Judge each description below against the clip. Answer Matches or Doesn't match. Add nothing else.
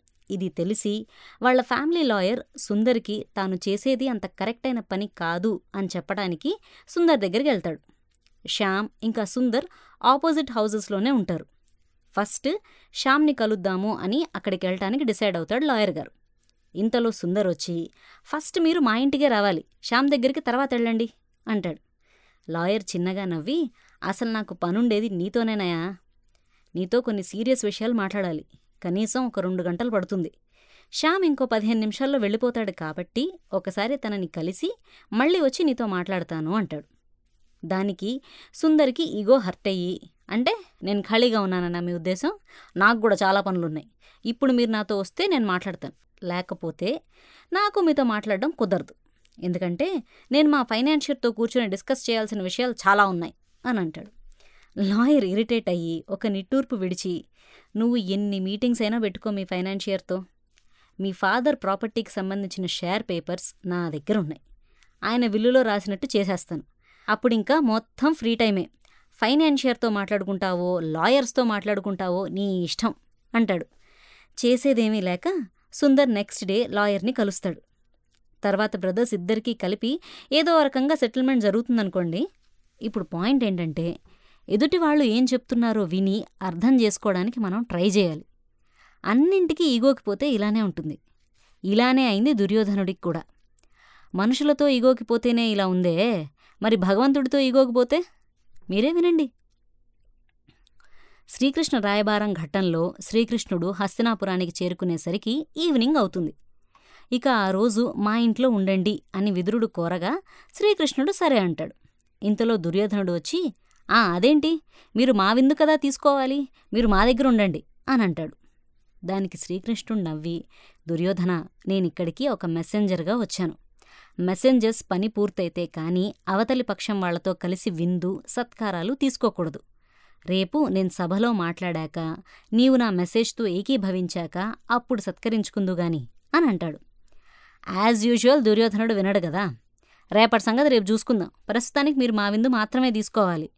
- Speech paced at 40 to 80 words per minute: Doesn't match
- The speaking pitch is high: Matches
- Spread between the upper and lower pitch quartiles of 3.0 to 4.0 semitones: Doesn't match